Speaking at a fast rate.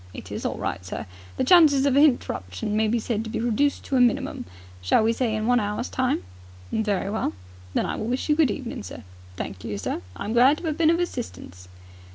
Yes: fast, 230 wpm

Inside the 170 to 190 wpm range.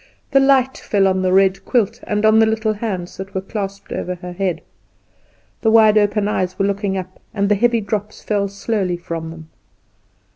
Yes: average, 185 wpm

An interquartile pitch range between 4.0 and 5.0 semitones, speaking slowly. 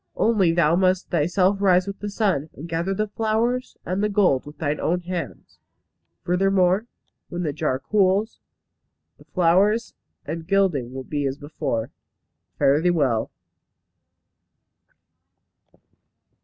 Yes: average, 4.5 semitones; slow, 130 wpm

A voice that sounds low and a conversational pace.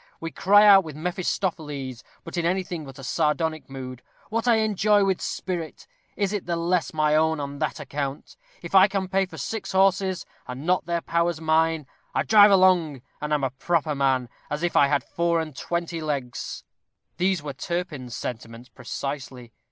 No: medium, 165 Hz; average, 180 wpm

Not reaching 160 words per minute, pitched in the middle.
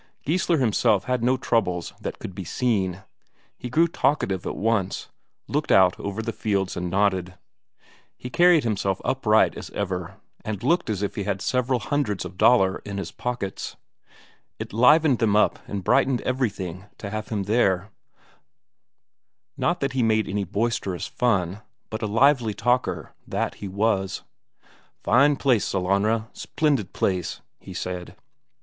No: average, 150 wpm; low, 105 Hz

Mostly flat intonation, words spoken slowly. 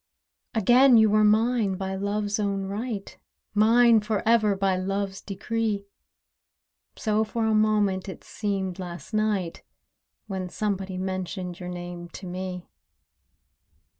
Yes: narrow, 2.3 semitones; slow, 125 wpm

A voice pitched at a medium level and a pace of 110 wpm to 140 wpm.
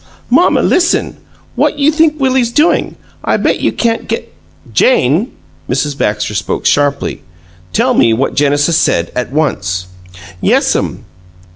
Yes: medium, 145 Hz; slow, 135 wpm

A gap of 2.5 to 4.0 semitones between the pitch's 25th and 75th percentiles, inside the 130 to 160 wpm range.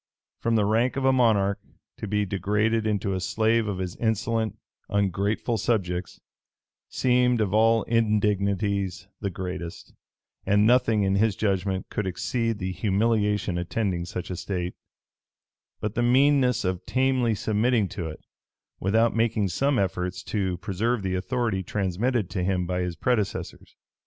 Yes: average, 3.4 semitones; average, 145 wpm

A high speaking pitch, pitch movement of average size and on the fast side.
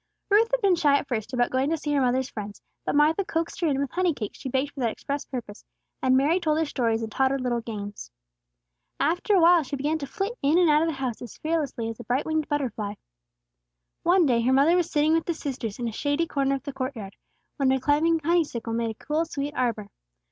Yes: very high, 280 Hz; average, 4.7 semitones; fast, 245 wpm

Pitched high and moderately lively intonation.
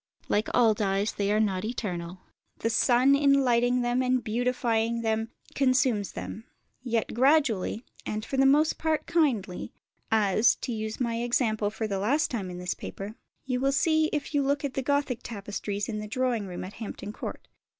Yes: high, 230 Hz; average, 3.9 semitones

